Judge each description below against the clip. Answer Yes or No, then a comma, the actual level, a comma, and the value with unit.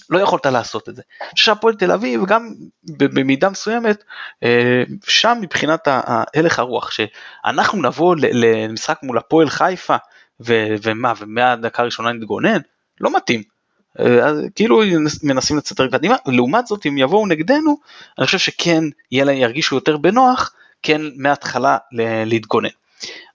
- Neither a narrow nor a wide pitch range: No, wide, 8.0 semitones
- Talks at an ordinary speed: Yes, average, 140 wpm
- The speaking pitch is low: No, medium, 145 Hz